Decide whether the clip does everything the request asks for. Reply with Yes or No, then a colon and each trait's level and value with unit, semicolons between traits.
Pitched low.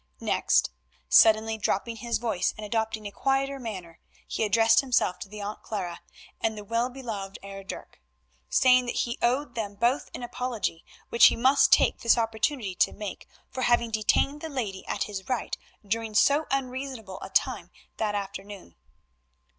No: high, 225 Hz